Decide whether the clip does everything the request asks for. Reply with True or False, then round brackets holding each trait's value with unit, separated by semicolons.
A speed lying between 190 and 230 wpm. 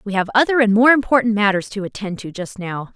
False (245 wpm)